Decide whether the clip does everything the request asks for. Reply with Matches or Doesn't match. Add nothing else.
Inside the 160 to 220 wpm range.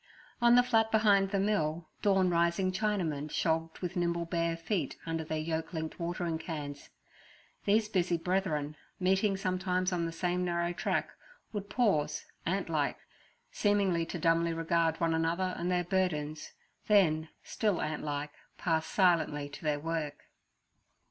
Doesn't match